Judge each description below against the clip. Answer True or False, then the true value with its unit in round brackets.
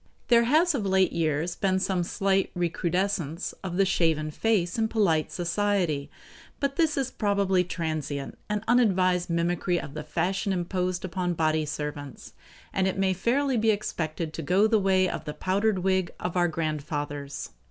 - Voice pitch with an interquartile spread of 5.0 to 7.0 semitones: False (3.7 semitones)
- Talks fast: False (165 wpm)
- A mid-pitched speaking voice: True (180 Hz)